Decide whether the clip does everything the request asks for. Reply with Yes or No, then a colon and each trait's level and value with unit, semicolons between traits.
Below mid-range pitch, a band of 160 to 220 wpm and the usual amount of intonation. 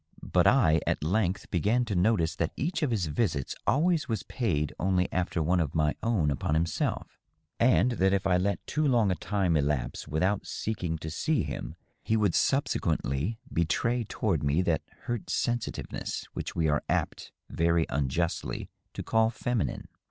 No: very low, 90 Hz; average, 165 wpm; wide, 5.8 semitones